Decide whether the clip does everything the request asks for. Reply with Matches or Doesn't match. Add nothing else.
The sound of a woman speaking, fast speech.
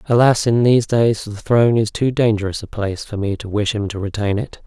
Doesn't match